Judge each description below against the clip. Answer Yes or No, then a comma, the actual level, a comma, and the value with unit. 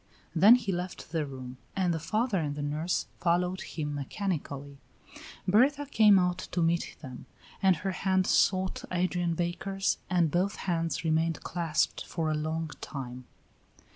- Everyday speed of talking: Yes, average, 150 wpm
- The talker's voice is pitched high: No, medium, 175 Hz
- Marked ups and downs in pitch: No, average, 3.4 semitones